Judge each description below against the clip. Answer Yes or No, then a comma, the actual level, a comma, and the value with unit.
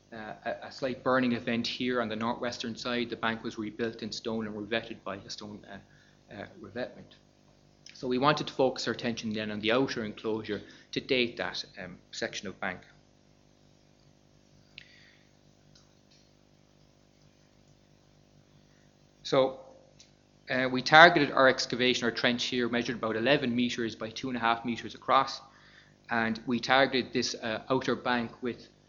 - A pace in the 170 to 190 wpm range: No, average, 150 wpm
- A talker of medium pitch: No, low, 120 Hz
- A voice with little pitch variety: Yes, narrow, 2.3 semitones